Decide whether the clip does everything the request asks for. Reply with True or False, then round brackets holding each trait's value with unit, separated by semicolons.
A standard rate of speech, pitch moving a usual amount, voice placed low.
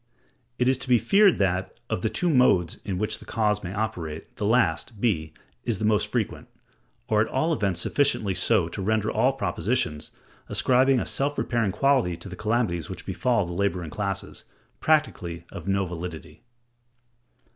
False (170 wpm; 5.7 semitones; 105 Hz)